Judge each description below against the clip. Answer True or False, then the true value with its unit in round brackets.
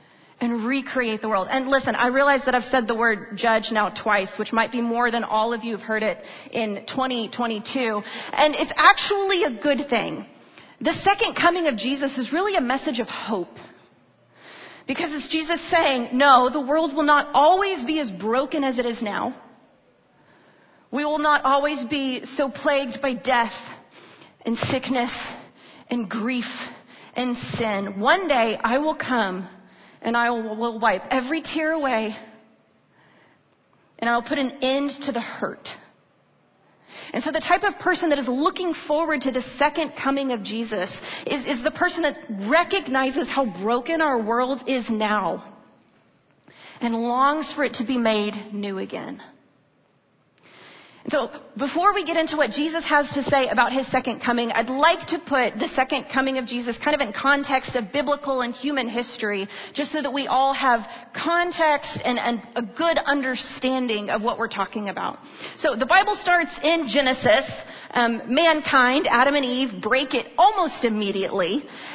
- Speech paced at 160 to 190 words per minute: True (165 wpm)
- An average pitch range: True (3.9 semitones)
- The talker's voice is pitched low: False (260 Hz)